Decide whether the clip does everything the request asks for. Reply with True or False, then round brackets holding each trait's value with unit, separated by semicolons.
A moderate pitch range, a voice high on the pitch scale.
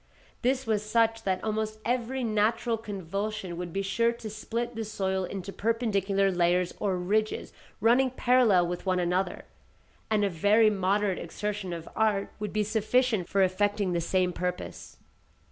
True (3.2 semitones; 205 Hz)